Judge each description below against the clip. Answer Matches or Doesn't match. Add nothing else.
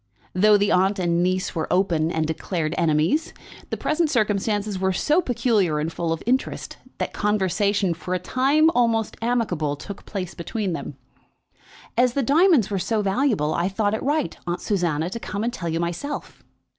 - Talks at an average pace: Matches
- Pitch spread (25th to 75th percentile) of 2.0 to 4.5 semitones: Doesn't match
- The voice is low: Doesn't match